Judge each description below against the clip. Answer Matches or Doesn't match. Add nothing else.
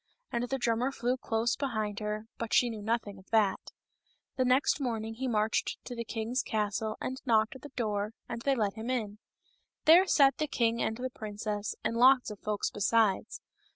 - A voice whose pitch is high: Matches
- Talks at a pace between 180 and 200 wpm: Matches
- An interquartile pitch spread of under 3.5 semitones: Matches